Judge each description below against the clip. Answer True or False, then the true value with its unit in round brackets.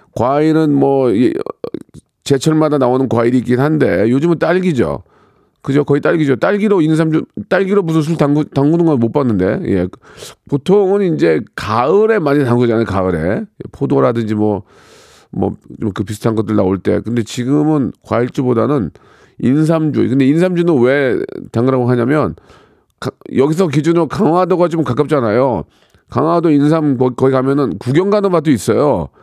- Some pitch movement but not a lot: True (4.9 semitones)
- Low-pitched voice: False (145 Hz)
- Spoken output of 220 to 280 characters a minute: False (315 characters per minute)